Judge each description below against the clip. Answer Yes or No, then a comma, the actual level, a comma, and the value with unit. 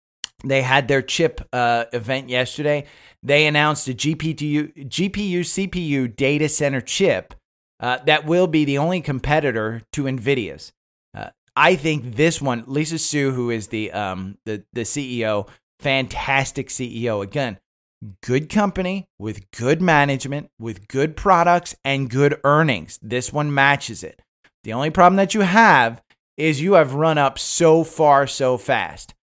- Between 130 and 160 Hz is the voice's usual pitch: Yes, medium, 140 Hz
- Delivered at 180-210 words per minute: No, average, 150 wpm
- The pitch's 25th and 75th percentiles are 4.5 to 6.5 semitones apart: No, average, 4.1 semitones